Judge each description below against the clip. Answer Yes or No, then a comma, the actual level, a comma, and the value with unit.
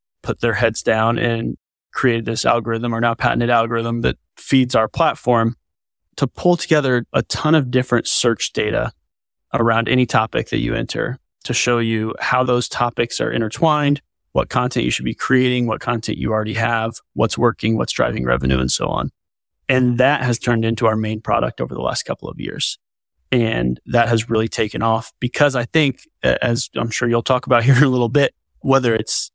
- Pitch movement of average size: No, narrow, 2.1 semitones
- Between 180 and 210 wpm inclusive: Yes, average, 190 wpm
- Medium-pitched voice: No, low, 115 Hz